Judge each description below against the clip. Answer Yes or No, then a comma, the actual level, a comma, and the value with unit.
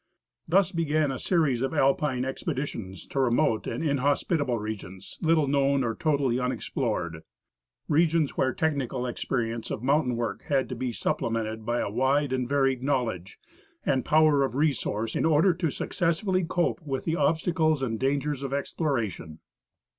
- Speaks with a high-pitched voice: No, low, 135 Hz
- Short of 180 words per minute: Yes, average, 155 wpm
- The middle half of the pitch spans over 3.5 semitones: Yes, average, 4.4 semitones